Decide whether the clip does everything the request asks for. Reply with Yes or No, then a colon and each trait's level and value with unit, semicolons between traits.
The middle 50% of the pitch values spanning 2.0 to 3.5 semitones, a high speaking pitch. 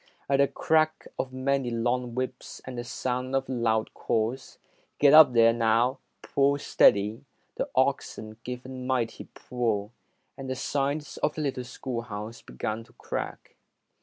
No: average, 2.7 semitones; low, 125 Hz